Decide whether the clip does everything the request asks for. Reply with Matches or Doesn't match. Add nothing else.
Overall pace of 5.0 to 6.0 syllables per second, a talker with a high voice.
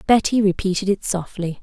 Matches